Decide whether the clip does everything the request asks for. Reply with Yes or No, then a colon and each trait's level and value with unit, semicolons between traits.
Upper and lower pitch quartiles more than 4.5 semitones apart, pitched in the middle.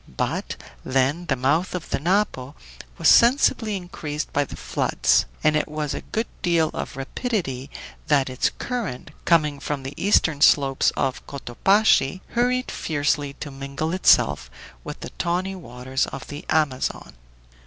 Yes: average, 5.1 semitones; medium, 150 Hz